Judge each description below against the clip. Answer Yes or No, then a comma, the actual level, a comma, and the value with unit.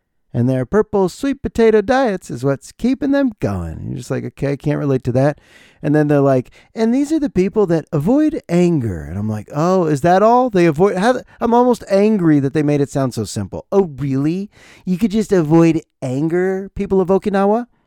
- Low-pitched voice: No, medium, 175 Hz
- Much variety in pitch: Yes, wide, 7.6 semitones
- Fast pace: Yes, fast, 210 wpm